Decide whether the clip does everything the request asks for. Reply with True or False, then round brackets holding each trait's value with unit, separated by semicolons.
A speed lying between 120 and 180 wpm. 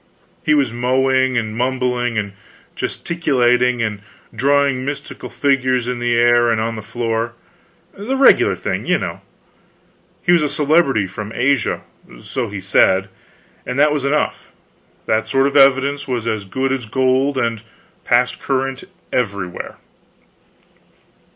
True (140 wpm)